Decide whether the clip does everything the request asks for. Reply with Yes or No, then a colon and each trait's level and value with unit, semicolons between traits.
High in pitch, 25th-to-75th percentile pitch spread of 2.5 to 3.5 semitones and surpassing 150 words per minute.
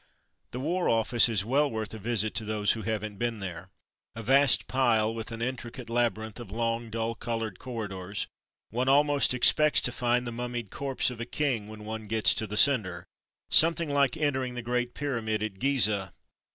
No: low, 115 Hz; average, 2.9 semitones; average, 190 wpm